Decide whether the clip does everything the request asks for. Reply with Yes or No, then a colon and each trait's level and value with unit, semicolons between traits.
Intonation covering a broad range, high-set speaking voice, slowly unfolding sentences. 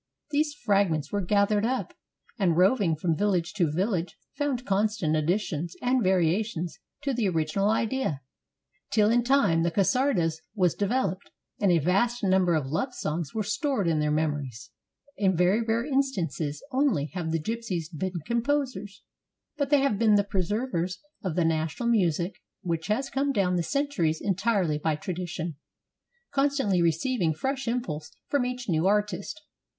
No: wide, 6.3 semitones; high, 195 Hz; average, 155 wpm